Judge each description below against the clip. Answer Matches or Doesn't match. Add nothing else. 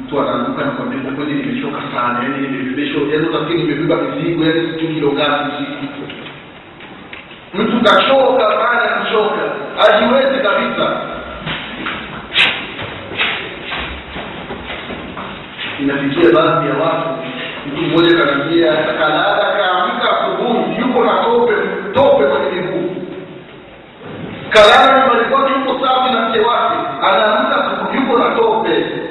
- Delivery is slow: Doesn't match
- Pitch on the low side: Doesn't match